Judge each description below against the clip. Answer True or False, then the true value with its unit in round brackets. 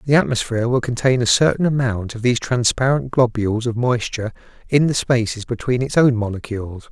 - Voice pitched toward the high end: False (120 Hz)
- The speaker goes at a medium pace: True (175 wpm)